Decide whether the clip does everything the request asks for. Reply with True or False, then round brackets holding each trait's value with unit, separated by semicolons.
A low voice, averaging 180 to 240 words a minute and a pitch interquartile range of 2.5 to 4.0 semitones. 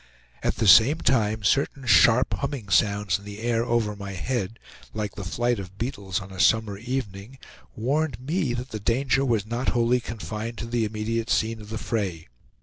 True (115 Hz; 185 wpm; 2.9 semitones)